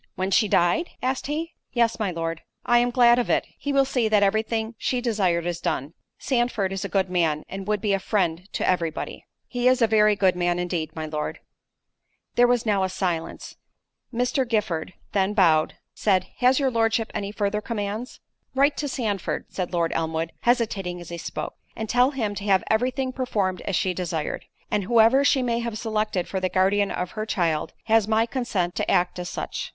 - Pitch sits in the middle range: No, high, 205 Hz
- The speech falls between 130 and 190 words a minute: No, average, 200 wpm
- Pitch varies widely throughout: No, average, 4.9 semitones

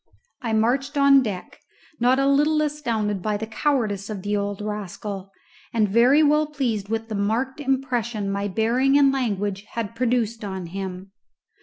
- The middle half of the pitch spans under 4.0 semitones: No, average, 4.8 semitones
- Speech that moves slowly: No, average, 160 wpm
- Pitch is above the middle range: Yes, high, 225 Hz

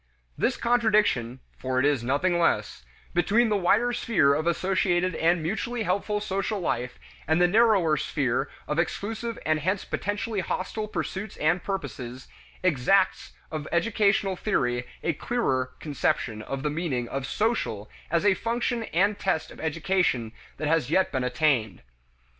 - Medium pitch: Yes, medium, 175 Hz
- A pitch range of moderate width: No, wide, 6.7 semitones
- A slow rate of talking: No, average, 145 wpm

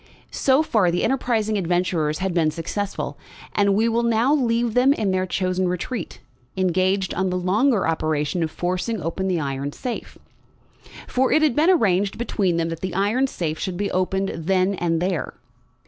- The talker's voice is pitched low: No, high, 190 Hz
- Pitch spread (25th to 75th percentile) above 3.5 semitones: Yes, average, 4.5 semitones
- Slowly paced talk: No, average, 175 wpm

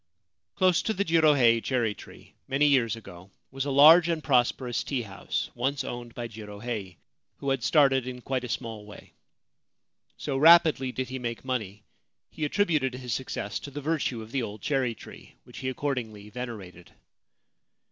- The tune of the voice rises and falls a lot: No, average, 3.8 semitones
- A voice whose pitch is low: Yes, low, 130 Hz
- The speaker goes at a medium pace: Yes, average, 165 wpm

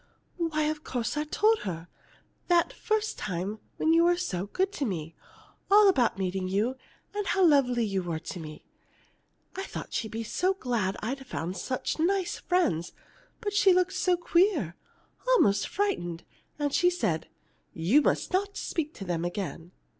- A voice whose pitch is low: No, very high, 275 Hz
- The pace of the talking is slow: No, average, 165 wpm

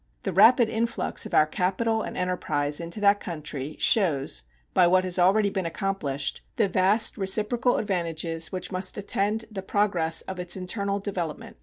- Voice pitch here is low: No, medium, 185 Hz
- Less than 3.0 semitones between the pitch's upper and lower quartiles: No, average, 3.5 semitones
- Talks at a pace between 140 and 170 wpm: Yes, average, 160 wpm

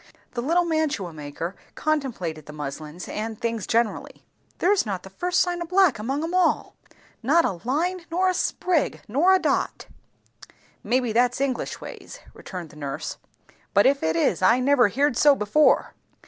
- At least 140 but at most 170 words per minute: Yes, average, 165 wpm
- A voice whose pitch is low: No, very high, 250 Hz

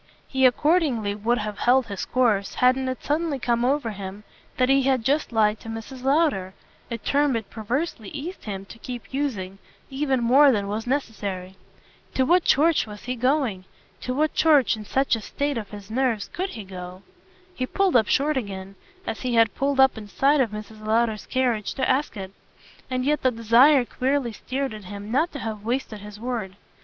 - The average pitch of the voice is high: Yes, high, 245 Hz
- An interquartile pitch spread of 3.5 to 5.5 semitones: Yes, average, 4.3 semitones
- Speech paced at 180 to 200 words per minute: Yes, average, 195 wpm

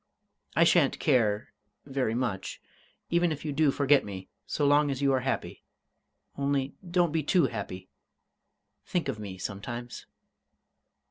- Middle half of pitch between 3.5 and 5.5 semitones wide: Yes, average, 5.1 semitones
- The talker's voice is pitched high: No, low, 135 Hz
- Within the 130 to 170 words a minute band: Yes, average, 140 wpm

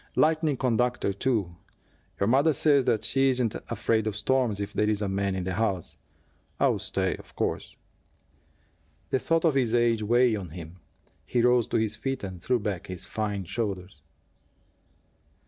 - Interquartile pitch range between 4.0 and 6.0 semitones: Yes, average, 4.4 semitones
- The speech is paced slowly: No, average, 165 wpm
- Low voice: Yes, low, 110 Hz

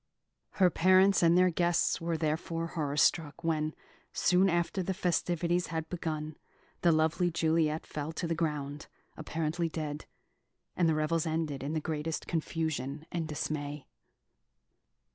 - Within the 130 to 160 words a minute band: Yes, average, 140 wpm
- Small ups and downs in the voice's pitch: Yes, narrow, 1.9 semitones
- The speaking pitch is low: No, medium, 160 Hz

